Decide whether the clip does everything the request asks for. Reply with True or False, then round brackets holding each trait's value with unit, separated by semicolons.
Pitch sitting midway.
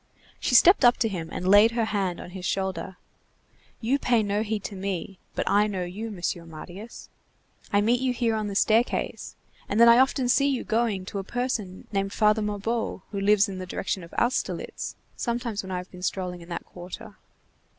False (205 Hz)